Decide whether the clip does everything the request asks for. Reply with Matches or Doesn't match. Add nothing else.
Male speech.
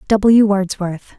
Doesn't match